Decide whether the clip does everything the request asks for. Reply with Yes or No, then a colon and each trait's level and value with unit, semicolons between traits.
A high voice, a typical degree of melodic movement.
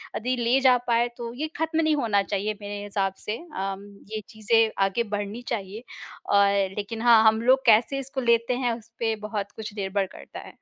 Yes: high, 225 Hz; average, 3.0 semitones